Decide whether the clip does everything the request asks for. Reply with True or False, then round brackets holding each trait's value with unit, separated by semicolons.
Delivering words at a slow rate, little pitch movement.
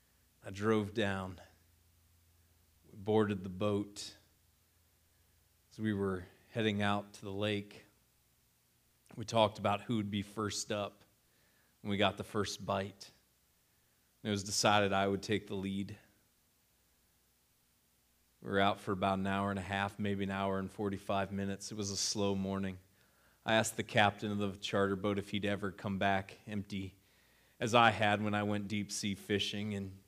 False (165 wpm; 2.1 semitones)